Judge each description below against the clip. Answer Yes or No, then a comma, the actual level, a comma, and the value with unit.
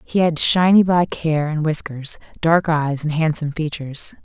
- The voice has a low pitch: No, medium, 155 Hz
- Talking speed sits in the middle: Yes, average, 170 wpm